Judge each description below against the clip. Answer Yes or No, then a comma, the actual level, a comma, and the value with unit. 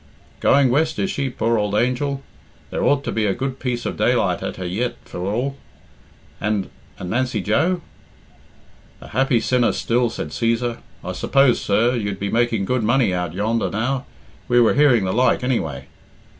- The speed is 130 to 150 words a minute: No, average, 175 wpm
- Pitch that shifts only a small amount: No, average, 3.8 semitones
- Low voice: Yes, low, 120 Hz